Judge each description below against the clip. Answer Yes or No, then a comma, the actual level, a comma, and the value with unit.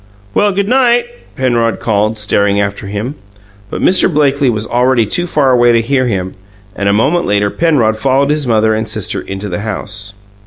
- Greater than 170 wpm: Yes, average, 185 wpm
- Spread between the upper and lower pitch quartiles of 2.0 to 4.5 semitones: No, average, 5.2 semitones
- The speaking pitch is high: No, low, 115 Hz